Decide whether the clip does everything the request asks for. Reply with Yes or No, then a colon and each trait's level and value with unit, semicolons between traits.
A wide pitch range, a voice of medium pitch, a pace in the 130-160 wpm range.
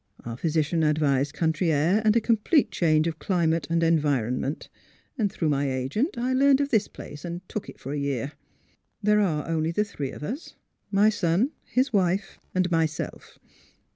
No: wide, 5.9 semitones; medium, 165 Hz; average, 175 wpm